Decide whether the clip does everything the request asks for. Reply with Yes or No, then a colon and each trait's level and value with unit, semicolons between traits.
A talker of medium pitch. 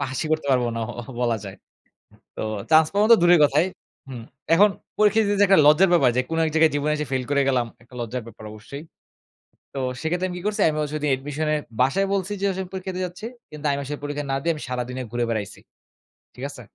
Yes: medium, 150 Hz